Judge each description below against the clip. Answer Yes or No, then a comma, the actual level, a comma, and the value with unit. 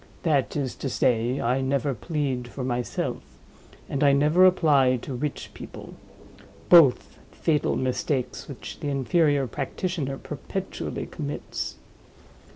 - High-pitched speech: No, medium, 140 Hz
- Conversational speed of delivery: No, slow, 115 wpm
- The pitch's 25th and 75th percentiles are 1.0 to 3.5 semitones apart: Yes, average, 2.7 semitones